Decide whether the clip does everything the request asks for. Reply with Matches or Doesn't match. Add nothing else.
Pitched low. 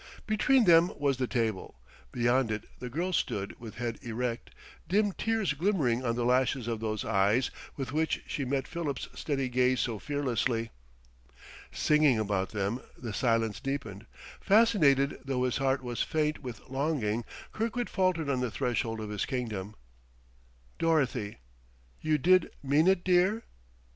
Matches